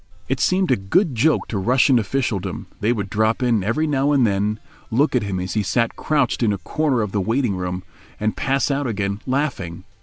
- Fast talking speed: Yes, fast, 210 wpm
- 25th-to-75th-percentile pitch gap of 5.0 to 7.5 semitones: Yes, wide, 5.4 semitones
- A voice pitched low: Yes, low, 115 Hz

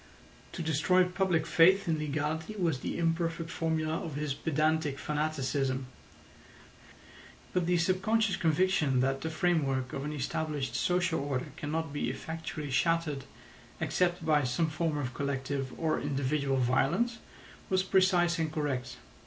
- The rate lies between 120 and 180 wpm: Yes, slow, 135 wpm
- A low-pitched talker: No, medium, 155 Hz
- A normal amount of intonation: Yes, average, 3.3 semitones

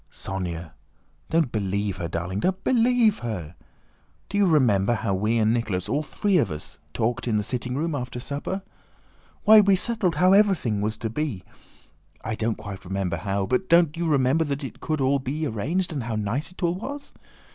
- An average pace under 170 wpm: No, average, 190 wpm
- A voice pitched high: No, low, 125 Hz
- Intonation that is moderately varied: No, wide, 8.6 semitones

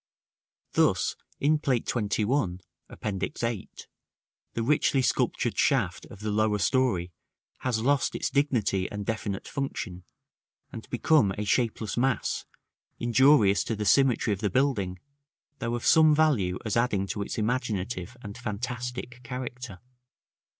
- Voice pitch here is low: Yes, low, 115 Hz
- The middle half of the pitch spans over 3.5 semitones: Yes, average, 4.0 semitones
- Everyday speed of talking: No, slow, 130 wpm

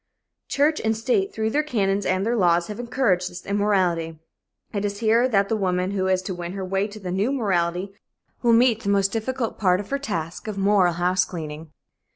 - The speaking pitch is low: No, high, 200 Hz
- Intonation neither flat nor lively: Yes, average, 3.5 semitones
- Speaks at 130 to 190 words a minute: No, fast, 205 wpm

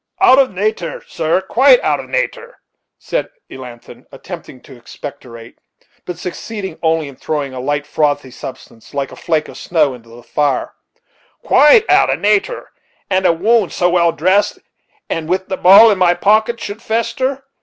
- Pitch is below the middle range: No, medium, 175 Hz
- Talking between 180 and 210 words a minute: No, average, 165 wpm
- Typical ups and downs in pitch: No, wide, 6.9 semitones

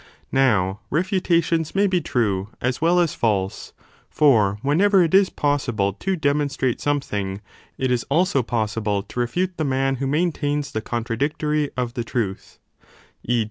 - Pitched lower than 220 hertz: Yes, low, 135 Hz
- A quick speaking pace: No, average, 145 wpm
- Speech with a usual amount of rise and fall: No, wide, 5.8 semitones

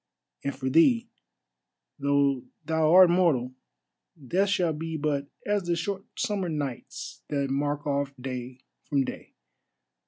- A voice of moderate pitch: Yes, medium, 150 Hz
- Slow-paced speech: Yes, slow, 130 wpm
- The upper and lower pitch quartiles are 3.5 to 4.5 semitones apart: Yes, average, 4.0 semitones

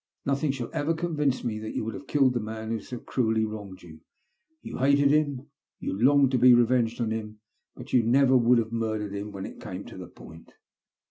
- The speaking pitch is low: Yes, low, 120 Hz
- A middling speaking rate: No, fast, 215 wpm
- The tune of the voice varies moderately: Yes, average, 3.8 semitones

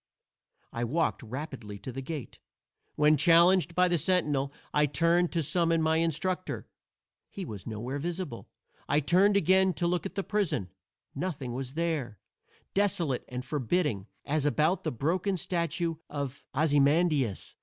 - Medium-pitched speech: Yes, medium, 155 Hz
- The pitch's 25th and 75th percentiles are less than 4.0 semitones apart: No, average, 4.6 semitones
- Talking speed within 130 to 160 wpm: Yes, average, 145 wpm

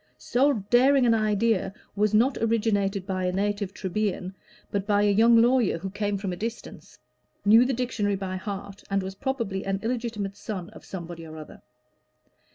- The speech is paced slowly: No, average, 170 wpm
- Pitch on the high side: Yes, high, 205 Hz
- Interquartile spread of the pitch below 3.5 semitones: Yes, average, 3.0 semitones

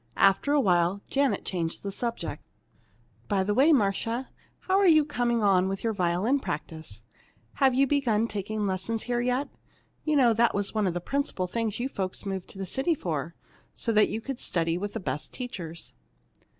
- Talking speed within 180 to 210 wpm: Yes, average, 190 wpm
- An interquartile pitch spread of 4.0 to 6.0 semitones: Yes, average, 5.3 semitones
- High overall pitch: Yes, high, 210 Hz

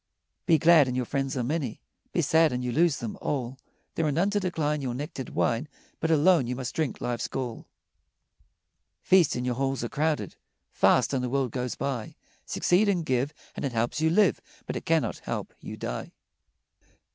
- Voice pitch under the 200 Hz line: Yes, low, 135 Hz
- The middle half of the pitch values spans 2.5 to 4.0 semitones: No, average, 4.4 semitones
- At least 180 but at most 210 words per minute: Yes, average, 190 wpm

